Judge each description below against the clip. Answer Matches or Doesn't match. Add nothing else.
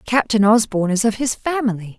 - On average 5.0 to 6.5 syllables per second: Matches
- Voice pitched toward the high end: Matches